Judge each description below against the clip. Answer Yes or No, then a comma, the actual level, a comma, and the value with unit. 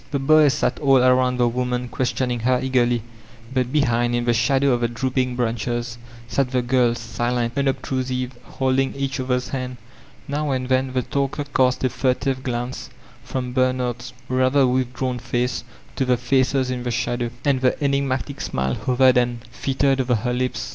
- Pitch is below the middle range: Yes, low, 125 Hz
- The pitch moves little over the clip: Yes, narrow, 1.4 semitones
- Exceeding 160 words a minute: Yes, average, 170 wpm